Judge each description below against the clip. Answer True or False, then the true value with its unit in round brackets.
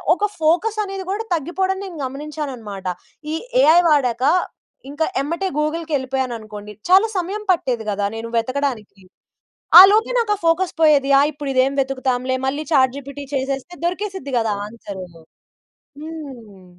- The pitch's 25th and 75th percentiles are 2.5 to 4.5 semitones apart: False (5.5 semitones)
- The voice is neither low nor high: False (280 Hz)